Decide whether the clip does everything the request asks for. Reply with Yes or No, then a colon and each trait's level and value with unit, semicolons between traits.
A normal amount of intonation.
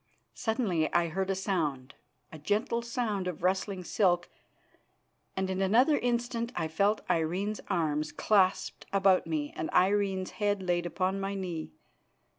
Yes: average, 3.0 semitones